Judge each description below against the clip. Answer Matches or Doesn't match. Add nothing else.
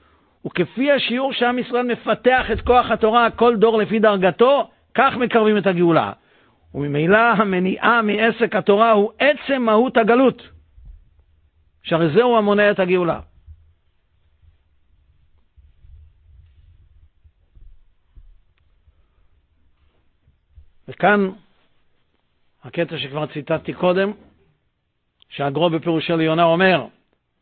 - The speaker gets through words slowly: Matches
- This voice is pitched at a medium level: Matches